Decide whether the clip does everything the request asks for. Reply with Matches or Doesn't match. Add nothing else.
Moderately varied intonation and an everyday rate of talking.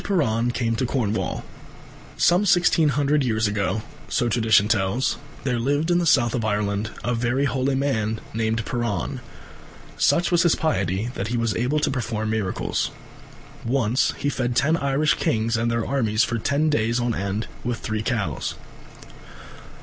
Matches